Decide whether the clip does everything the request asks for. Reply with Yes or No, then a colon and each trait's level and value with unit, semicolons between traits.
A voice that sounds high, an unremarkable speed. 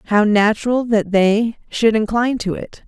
Yes: high, 220 Hz; average, 165 wpm